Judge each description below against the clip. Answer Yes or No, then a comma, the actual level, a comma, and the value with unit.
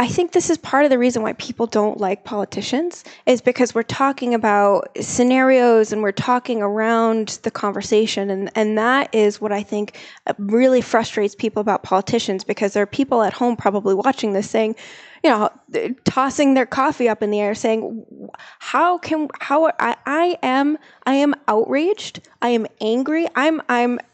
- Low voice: No, high, 230 Hz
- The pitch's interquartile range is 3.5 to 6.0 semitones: Yes, average, 3.9 semitones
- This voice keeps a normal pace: Yes, average, 175 wpm